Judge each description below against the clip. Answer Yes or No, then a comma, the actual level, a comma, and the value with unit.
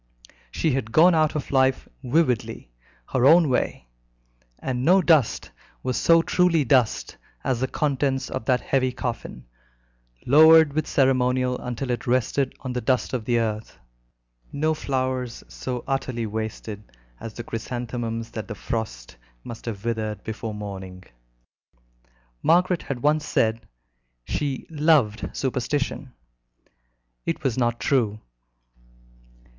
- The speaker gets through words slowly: Yes, slow, 130 wpm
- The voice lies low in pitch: Yes, low, 125 Hz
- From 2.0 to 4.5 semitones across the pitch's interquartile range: Yes, average, 3.6 semitones